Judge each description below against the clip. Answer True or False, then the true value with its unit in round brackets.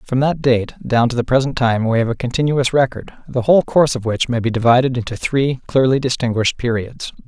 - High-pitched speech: False (125 Hz)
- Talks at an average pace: False (215 wpm)